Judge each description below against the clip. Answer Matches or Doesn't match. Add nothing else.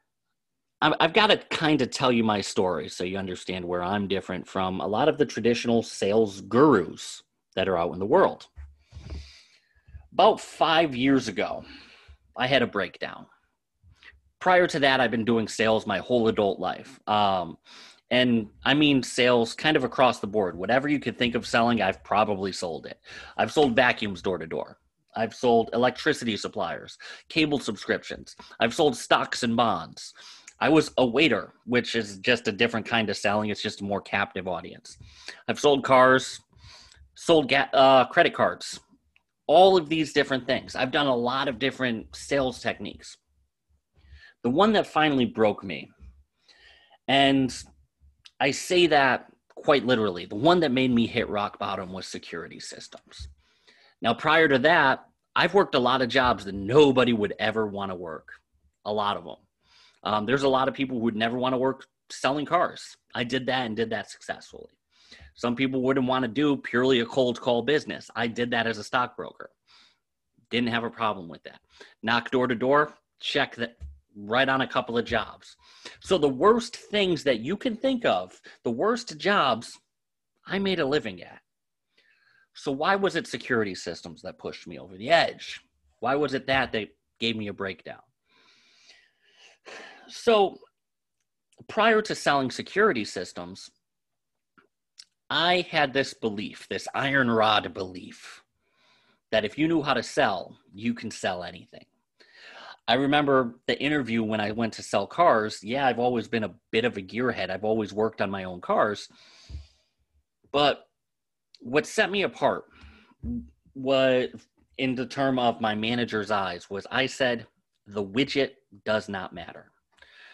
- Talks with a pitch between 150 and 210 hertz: Doesn't match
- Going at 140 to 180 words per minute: Matches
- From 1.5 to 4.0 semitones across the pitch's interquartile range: Doesn't match